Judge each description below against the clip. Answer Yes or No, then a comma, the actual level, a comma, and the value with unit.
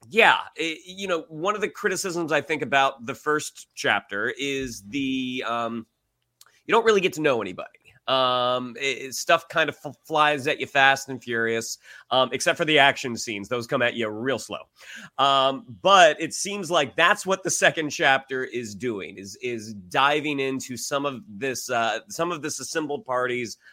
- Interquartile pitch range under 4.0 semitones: No, average, 4.5 semitones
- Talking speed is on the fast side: No, average, 185 wpm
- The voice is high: No, low, 135 Hz